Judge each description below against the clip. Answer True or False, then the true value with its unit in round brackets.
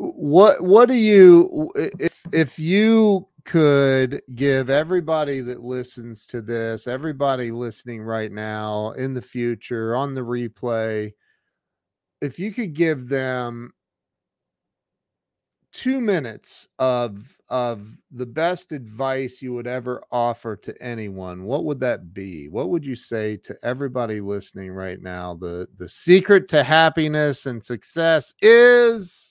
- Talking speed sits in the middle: False (130 wpm)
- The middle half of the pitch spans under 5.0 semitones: False (5.6 semitones)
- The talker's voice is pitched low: True (125 Hz)